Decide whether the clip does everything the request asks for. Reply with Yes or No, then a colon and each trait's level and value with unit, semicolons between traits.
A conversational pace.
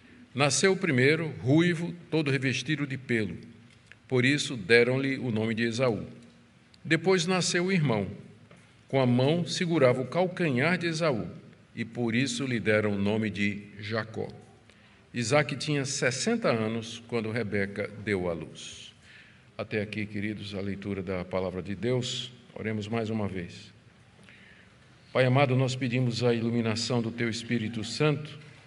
Yes: average, 140 wpm